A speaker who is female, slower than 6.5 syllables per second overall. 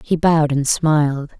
Yes: female; 4.9 syllables/s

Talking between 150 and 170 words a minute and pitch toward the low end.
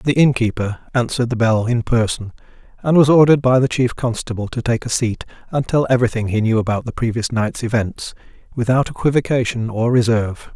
No: average, 180 wpm; low, 120 Hz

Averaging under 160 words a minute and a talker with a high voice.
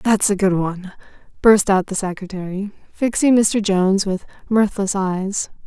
Yes: average, 150 wpm; high, 195 Hz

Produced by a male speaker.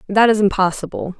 No: female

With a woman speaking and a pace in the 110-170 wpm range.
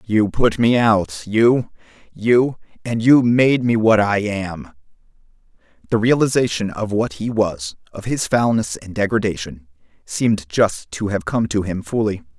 No: male; average, 145 wpm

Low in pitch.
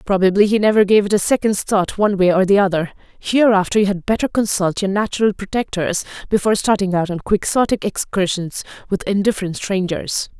No: high, 200 Hz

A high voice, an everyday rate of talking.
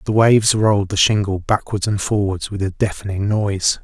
No: low, 100 Hz; average, 190 wpm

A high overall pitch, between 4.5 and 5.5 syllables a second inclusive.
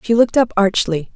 No: high, 210 Hz; 5.9 syllables/s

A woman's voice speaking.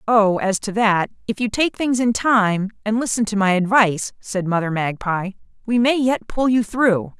Yes: female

